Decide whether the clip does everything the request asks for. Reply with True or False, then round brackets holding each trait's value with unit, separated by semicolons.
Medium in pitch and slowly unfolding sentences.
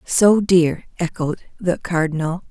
True (170 Hz; 120 wpm)